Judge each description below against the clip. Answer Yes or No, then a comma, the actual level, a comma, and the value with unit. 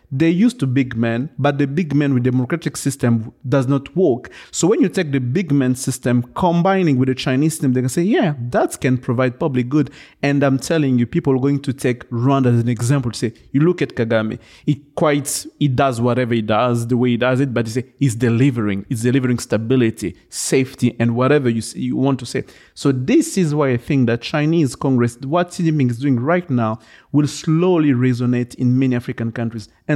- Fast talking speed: Yes, fast, 215 wpm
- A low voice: Yes, low, 130 Hz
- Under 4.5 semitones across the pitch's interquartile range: Yes, average, 3.1 semitones